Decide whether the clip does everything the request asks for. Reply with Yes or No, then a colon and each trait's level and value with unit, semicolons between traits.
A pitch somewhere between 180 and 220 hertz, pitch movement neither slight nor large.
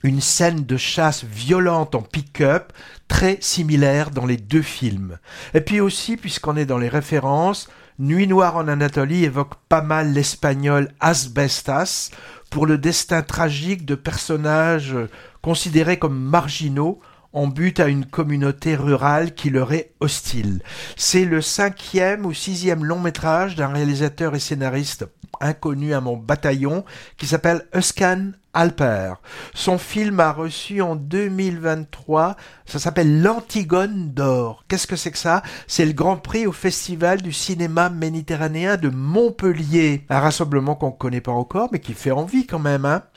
No: medium, 160 Hz; average, 3.8 semitones